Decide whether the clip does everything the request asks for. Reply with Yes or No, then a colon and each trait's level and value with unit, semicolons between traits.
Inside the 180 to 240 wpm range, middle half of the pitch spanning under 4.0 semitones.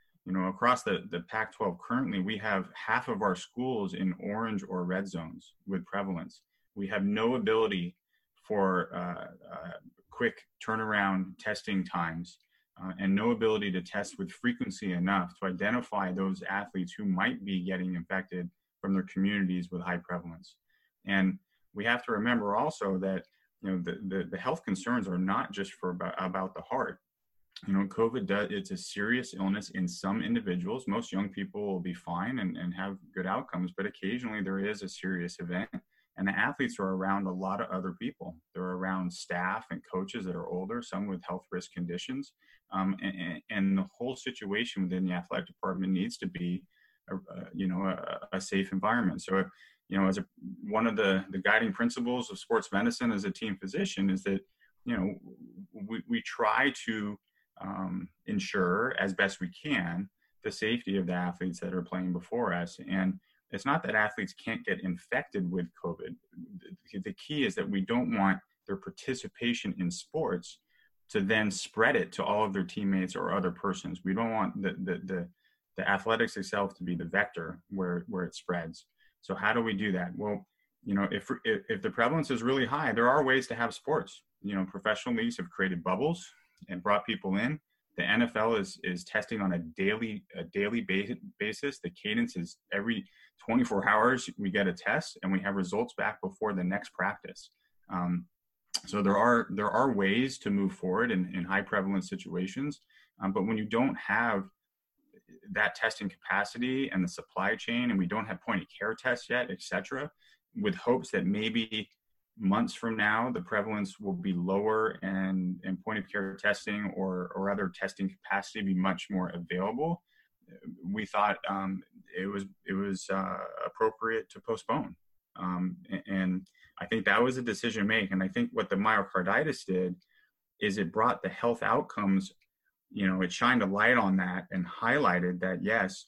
No: average, 185 wpm; average, 4.3 semitones